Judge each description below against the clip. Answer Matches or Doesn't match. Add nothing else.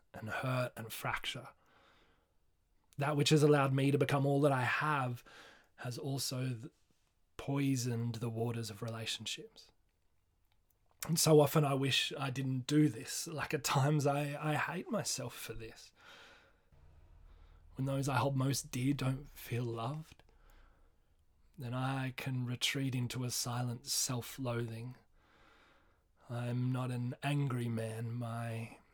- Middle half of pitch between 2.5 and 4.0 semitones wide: Matches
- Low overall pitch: Matches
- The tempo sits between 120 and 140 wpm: Matches